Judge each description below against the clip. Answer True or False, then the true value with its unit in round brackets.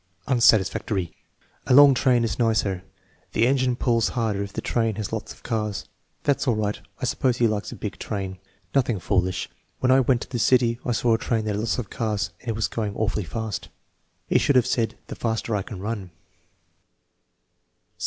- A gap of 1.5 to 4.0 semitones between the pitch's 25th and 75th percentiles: True (2.9 semitones)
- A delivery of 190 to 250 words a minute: True (195 wpm)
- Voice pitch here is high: False (115 Hz)